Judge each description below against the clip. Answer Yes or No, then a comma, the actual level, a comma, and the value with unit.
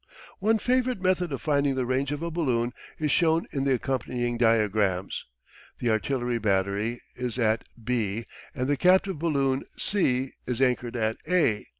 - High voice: No, low, 130 Hz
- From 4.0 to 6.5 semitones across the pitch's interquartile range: Yes, average, 4.9 semitones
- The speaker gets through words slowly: No, average, 160 wpm